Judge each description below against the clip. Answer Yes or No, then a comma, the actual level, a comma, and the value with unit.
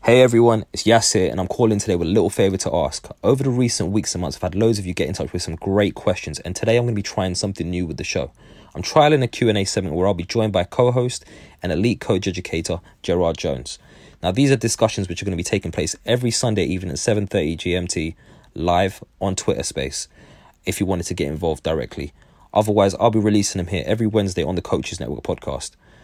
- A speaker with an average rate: No, fast, 235 wpm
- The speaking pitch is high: No, low, 100 Hz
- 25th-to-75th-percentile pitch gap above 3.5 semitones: Yes, average, 4.1 semitones